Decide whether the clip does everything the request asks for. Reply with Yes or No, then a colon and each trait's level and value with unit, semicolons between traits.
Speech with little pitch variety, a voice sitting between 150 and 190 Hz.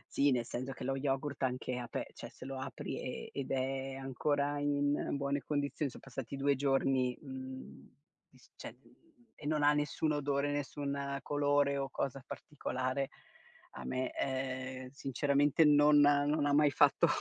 No: narrow, 1.6 semitones; medium, 140 Hz